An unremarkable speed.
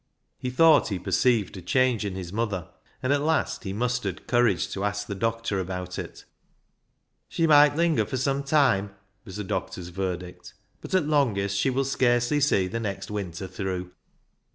Yes: average, 180 wpm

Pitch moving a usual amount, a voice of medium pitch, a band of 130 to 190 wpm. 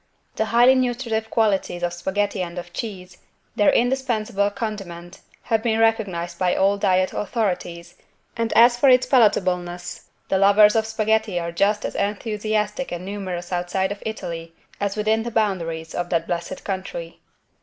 No: average, 3.8 semitones; high, 200 Hz; average, 155 wpm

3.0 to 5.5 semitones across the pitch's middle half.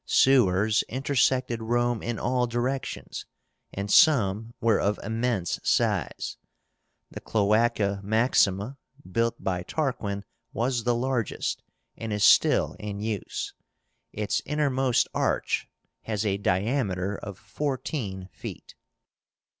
Yes: average, 3.8 semitones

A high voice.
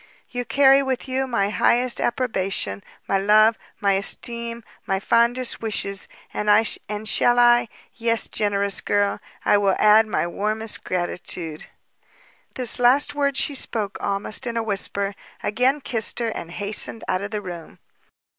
Yes: high, 215 Hz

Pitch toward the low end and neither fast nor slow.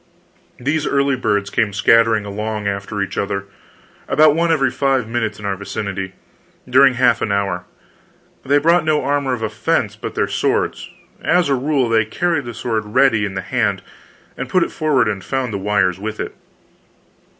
Yes: low, 115 Hz; average, 175 wpm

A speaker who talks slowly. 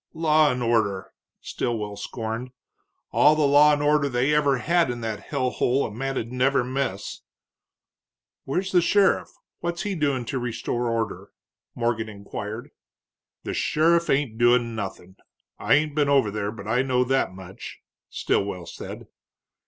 No: average, 150 wpm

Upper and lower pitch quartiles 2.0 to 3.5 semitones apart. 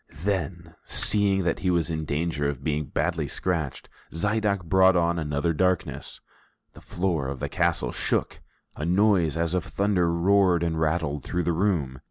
Yes: average, 3.0 semitones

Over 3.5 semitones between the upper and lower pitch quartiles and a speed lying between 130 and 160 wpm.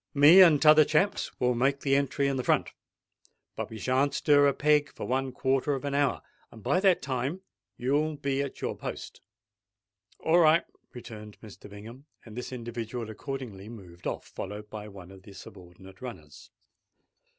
No: average, 5.0 semitones; average, 170 wpm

